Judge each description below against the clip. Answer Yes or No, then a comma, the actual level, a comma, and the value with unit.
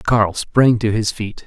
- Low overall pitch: Yes, low, 110 Hz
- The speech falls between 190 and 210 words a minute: Yes, fast, 205 wpm